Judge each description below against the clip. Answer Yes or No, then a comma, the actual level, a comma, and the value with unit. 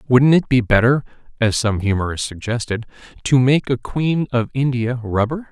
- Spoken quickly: No, average, 165 wpm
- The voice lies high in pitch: No, low, 125 Hz